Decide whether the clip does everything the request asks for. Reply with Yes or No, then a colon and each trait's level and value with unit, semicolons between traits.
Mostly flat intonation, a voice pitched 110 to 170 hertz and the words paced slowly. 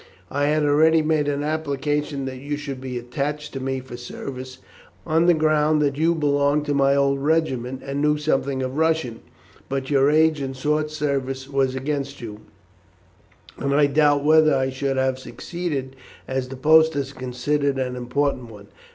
No: narrow, 2.2 semitones; medium, 140 Hz; average, 175 wpm